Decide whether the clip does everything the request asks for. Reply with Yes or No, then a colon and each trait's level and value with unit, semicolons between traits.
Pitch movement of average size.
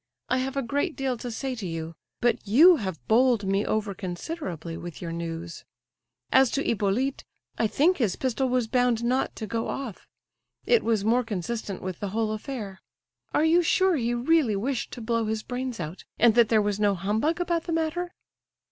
Yes: average, 5.0 semitones